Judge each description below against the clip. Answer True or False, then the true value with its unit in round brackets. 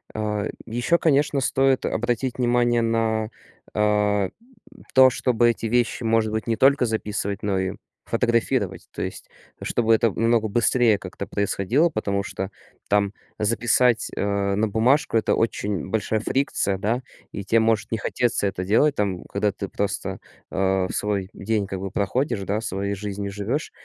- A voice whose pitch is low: True (110 Hz)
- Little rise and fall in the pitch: False (3.0 semitones)